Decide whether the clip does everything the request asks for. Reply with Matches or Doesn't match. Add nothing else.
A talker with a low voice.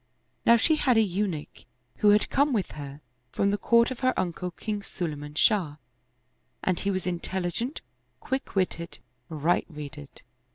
Doesn't match